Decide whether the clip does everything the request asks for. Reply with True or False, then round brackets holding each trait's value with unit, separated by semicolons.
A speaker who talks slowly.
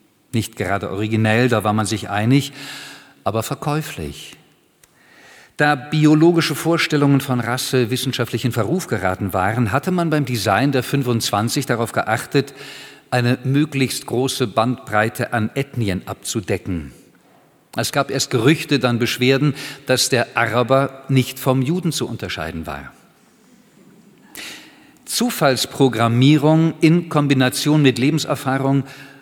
True (115 wpm)